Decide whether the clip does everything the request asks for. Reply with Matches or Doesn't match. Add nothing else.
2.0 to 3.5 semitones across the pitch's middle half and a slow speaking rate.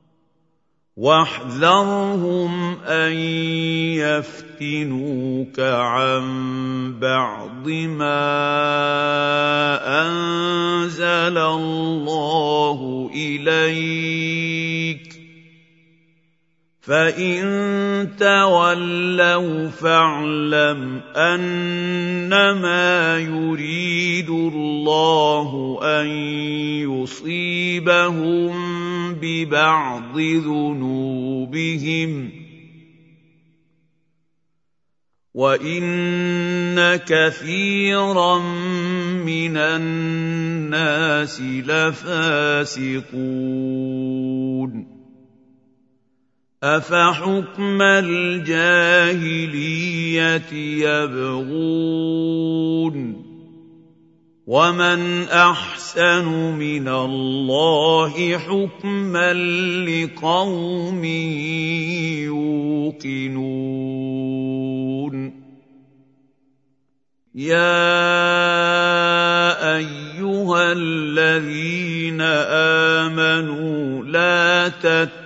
Matches